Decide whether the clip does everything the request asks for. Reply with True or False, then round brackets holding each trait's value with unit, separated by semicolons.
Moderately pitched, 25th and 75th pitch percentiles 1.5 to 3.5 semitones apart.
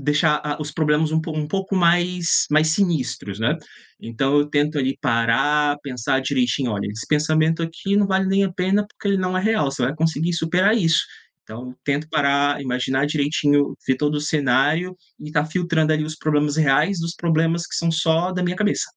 True (155 Hz; 3.2 semitones)